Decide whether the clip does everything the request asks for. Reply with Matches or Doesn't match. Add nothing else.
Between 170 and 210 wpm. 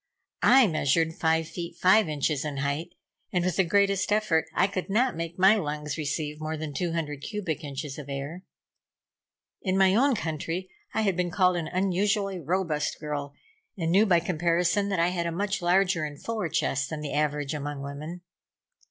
Matches